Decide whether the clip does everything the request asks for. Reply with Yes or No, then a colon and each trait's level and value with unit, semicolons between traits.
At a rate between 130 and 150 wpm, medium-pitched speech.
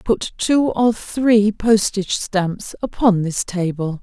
No: slow, 135 wpm; high, 205 Hz